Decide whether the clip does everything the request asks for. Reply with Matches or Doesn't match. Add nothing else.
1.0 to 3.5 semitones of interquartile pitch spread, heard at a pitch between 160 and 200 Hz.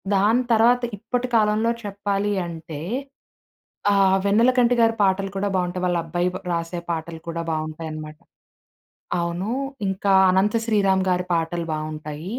Doesn't match